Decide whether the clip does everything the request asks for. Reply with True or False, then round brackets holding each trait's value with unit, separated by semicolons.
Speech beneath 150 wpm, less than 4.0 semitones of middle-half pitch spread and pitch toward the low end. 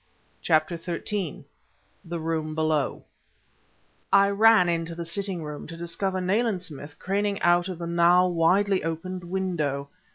False (135 wpm; 2.7 semitones; 175 Hz)